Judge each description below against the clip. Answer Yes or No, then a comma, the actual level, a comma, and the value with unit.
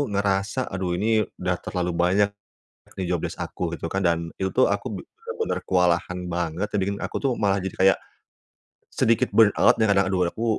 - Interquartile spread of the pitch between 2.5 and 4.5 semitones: Yes, average, 2.8 semitones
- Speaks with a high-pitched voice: No, very low, 95 Hz